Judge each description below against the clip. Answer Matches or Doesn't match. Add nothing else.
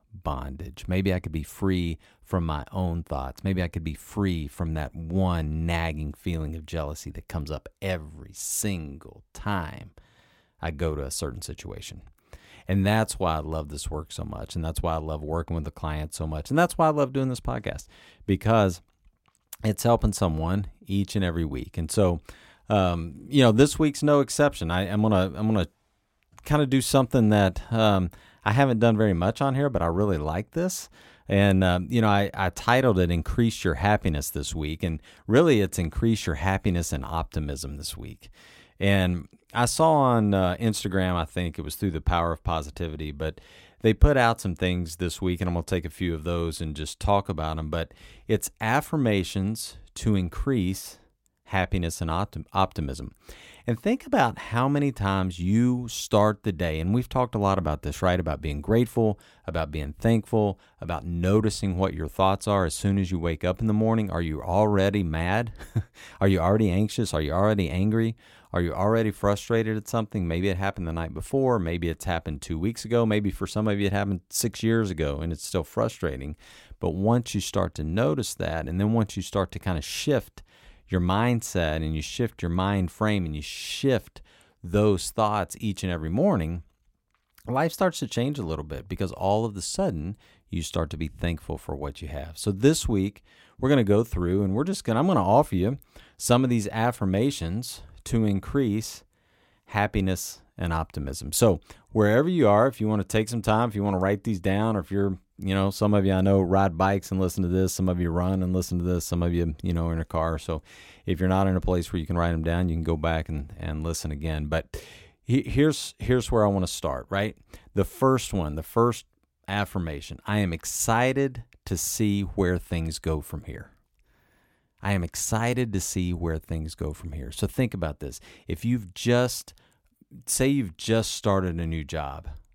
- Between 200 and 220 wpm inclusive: Matches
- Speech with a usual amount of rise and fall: Matches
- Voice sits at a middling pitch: Doesn't match